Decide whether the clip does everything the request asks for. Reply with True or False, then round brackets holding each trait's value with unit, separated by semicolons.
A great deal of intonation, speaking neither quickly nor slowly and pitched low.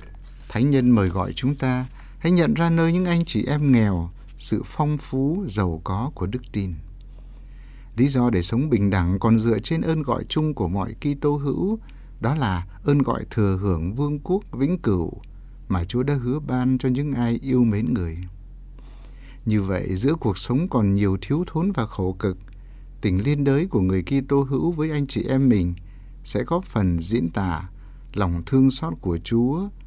True (6.0 semitones; 190 wpm; 125 Hz)